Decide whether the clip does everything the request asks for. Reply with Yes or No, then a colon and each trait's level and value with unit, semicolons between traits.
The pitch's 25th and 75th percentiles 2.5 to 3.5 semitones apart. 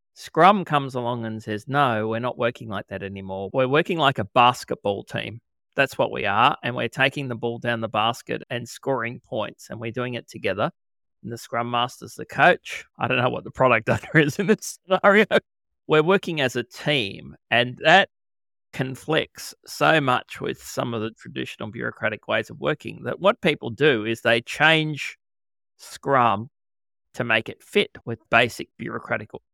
No: average, 4.7 semitones